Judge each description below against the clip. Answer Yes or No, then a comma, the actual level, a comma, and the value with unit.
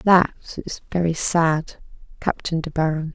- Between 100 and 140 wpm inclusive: Yes, slow, 135 wpm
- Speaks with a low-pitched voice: No, medium, 165 Hz